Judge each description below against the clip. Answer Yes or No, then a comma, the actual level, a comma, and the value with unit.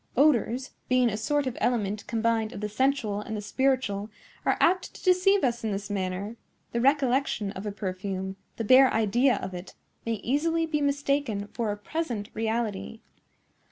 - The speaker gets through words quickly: No, average, 170 wpm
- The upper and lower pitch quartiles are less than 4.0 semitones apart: No, average, 4.9 semitones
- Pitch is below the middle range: No, high, 230 Hz